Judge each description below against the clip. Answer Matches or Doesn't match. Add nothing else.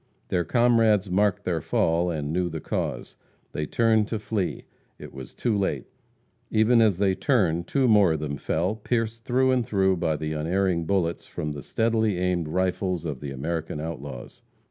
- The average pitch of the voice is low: Matches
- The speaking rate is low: Doesn't match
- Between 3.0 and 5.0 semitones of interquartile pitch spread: Doesn't match